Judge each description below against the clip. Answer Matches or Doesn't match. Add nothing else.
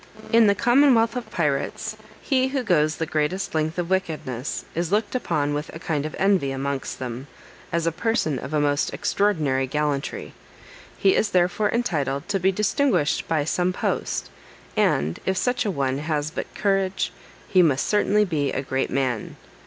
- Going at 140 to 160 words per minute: Doesn't match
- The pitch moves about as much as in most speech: Doesn't match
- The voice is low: Doesn't match